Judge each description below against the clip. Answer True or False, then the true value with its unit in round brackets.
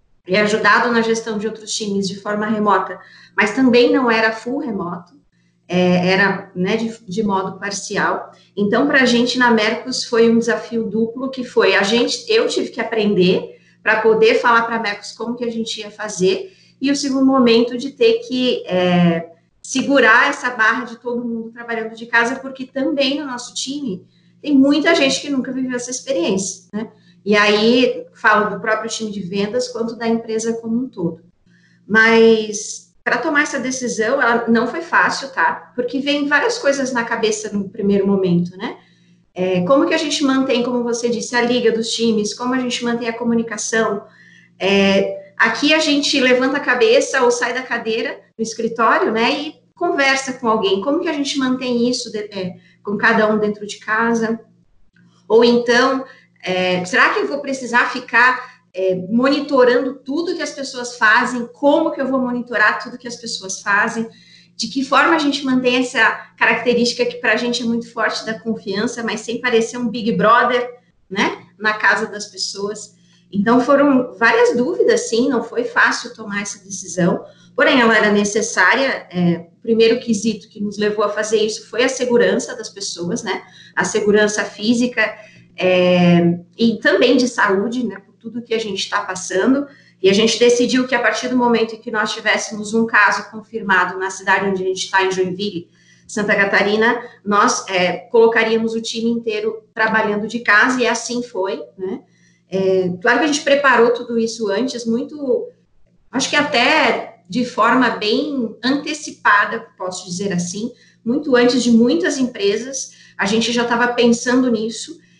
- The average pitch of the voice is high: True (230 Hz)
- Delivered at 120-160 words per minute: False (175 wpm)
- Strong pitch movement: False (3.2 semitones)